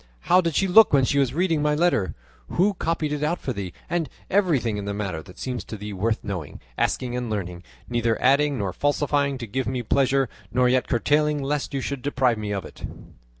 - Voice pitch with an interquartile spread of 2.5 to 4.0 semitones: No, wide, 5.4 semitones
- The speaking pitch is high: No, low, 130 Hz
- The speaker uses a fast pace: Yes, fast, 215 wpm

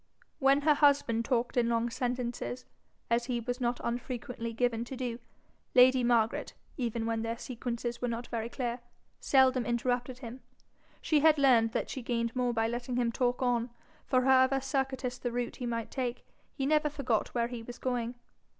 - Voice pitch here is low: No, high, 245 Hz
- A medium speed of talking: Yes, average, 175 wpm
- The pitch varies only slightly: Yes, narrow, 1.7 semitones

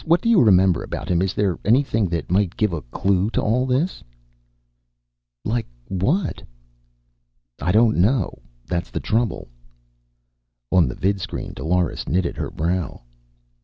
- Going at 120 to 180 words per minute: Yes, average, 140 wpm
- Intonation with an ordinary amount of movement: Yes, average, 4.6 semitones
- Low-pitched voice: Yes, very low, 95 Hz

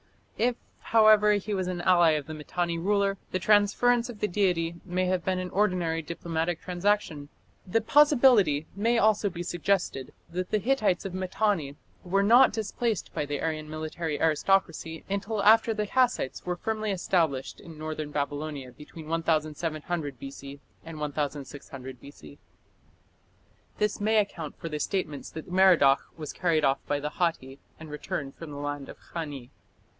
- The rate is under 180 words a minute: Yes, average, 155 wpm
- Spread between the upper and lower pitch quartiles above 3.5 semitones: Yes, average, 5.1 semitones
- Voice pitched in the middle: Yes, medium, 175 Hz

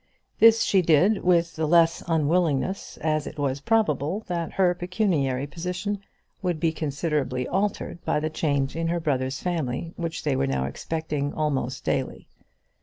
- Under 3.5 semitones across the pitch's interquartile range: No, average, 3.9 semitones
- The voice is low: No, medium, 160 Hz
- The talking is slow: No, average, 155 wpm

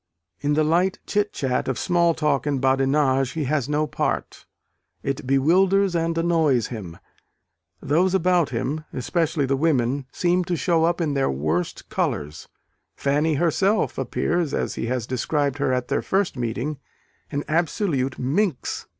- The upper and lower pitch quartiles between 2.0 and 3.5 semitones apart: No, average, 4.4 semitones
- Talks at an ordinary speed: Yes, average, 150 wpm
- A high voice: No, medium, 150 Hz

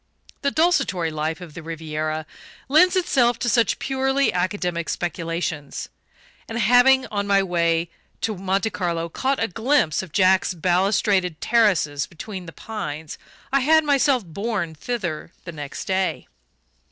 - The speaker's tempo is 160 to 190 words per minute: No, average, 140 wpm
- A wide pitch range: Yes, wide, 6.3 semitones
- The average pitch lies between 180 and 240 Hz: Yes, high, 190 Hz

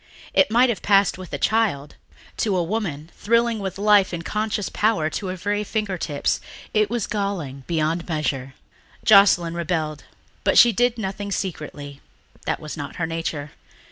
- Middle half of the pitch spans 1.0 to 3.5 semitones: No, average, 5.1 semitones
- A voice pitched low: No, medium, 185 Hz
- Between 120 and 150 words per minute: No, average, 160 wpm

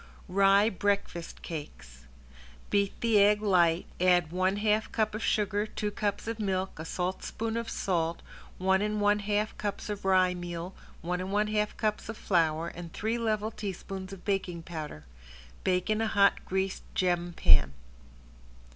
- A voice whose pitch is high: Yes, high, 195 Hz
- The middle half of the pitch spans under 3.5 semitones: Yes, average, 3.1 semitones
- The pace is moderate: Yes, average, 160 wpm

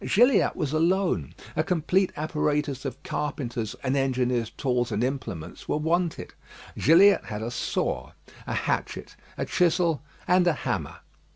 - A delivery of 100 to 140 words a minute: Yes, slow, 135 wpm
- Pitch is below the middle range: No, medium, 150 Hz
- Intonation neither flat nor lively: No, wide, 5.7 semitones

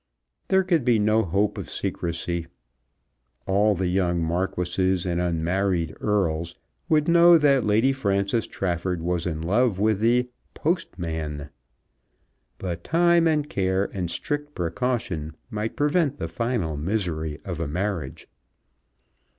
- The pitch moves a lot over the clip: Yes, wide, 6.3 semitones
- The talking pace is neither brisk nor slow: No, slow, 125 wpm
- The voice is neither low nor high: No, very low, 95 Hz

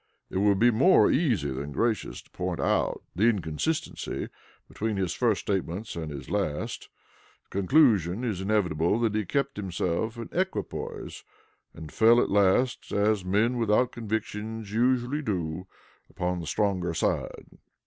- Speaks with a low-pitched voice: Yes, low, 105 Hz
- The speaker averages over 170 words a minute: No, average, 145 wpm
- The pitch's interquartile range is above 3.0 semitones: Yes, average, 4.6 semitones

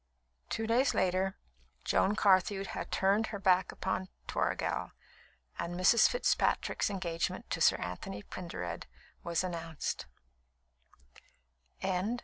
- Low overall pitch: No, medium, 185 Hz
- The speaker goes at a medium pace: No, slow, 105 wpm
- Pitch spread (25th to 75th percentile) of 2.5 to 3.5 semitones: Yes, average, 2.9 semitones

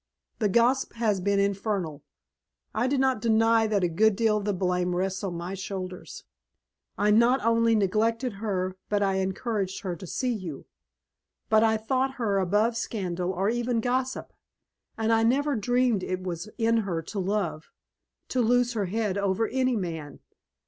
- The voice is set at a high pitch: Yes, high, 210 Hz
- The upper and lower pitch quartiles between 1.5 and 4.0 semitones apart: Yes, average, 3.5 semitones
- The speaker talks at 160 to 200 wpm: Yes, average, 170 wpm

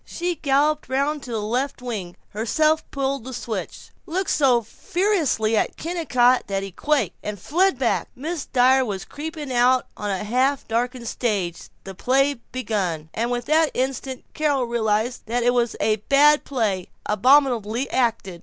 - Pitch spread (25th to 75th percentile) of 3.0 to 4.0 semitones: No, average, 4.5 semitones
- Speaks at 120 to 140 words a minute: No, average, 165 wpm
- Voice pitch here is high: Yes, very high, 250 Hz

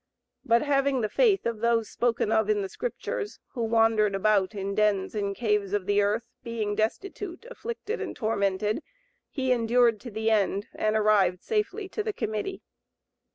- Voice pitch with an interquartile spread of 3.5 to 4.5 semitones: Yes, average, 3.8 semitones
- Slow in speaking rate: No, average, 165 wpm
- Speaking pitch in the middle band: No, high, 220 Hz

